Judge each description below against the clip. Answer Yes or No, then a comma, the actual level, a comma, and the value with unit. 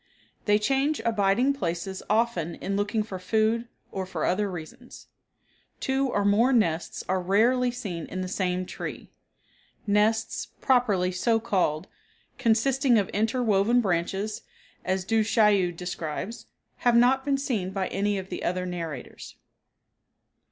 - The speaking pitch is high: Yes, high, 205 Hz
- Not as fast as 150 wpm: Yes, slow, 135 wpm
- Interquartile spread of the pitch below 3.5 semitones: No, average, 4.3 semitones